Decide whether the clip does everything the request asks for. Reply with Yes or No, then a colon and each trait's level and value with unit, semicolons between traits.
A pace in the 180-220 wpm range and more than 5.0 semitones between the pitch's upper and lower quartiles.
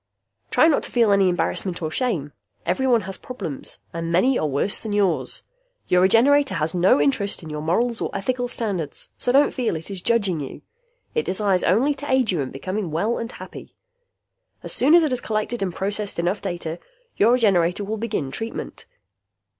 Yes: average, 185 wpm; wide, 5.6 semitones